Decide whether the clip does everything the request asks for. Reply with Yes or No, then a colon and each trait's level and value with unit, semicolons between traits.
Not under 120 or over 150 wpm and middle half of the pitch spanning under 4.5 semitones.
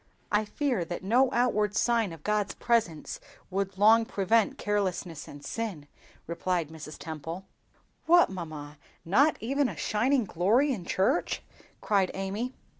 No: slow, 135 wpm; average, 5.1 semitones